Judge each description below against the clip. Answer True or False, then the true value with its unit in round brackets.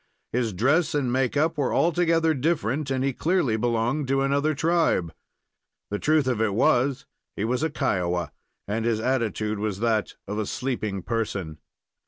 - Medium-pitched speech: False (125 Hz)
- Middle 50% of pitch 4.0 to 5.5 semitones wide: True (5.2 semitones)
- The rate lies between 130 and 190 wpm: True (165 wpm)